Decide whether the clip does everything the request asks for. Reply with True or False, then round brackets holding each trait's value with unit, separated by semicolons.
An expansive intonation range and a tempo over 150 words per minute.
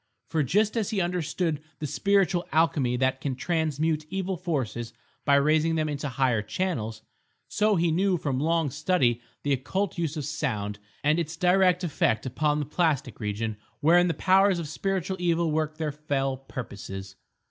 False (4.8 semitones; 165 wpm)